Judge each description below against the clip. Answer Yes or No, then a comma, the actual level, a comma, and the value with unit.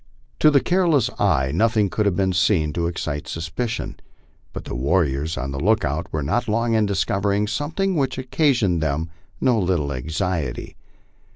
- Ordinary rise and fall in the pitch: No, wide, 6.7 semitones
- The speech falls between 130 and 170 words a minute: Yes, average, 165 wpm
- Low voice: Yes, very low, 95 Hz